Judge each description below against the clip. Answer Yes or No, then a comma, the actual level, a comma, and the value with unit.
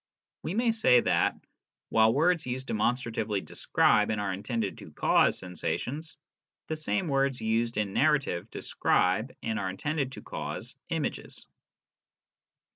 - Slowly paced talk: Yes, slow, 130 wpm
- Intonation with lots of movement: Yes, wide, 6.0 semitones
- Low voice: Yes, low, 120 Hz